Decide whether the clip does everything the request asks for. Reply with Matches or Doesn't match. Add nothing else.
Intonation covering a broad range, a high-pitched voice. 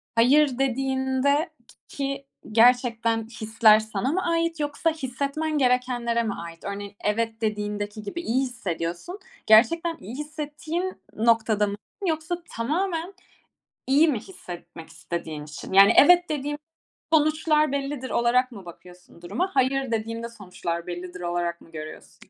Matches